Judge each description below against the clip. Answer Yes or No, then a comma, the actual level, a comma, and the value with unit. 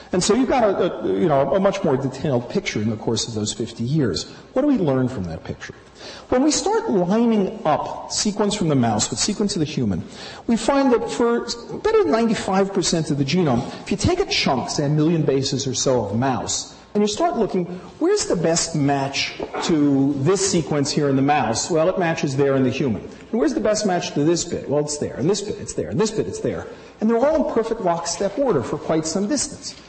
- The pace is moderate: No, fast, 235 wpm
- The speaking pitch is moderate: Yes, medium, 170 Hz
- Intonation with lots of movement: Yes, wide, 7.5 semitones